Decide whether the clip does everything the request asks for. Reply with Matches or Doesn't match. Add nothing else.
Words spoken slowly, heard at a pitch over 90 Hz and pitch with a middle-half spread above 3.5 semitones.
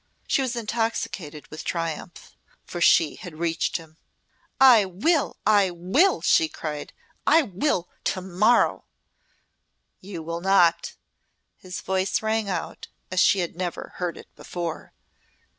Matches